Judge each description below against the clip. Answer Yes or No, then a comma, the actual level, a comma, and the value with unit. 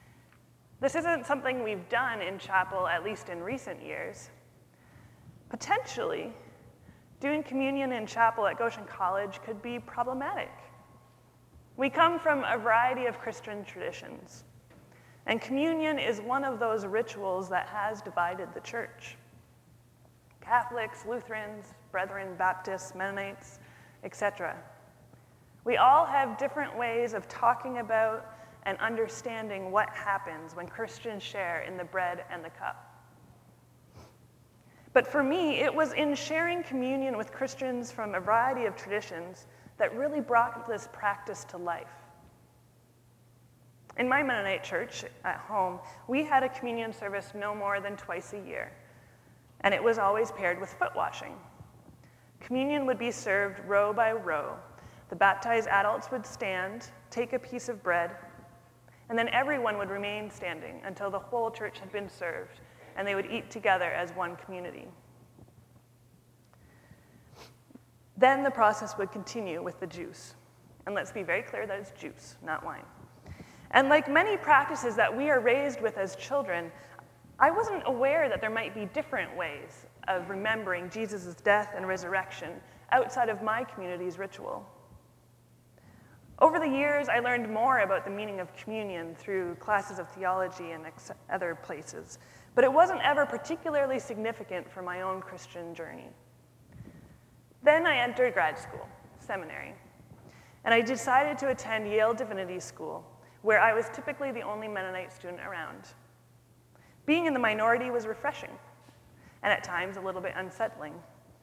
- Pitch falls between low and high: No, high, 210 Hz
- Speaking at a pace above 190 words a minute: No, average, 145 wpm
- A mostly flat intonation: No, average, 5.2 semitones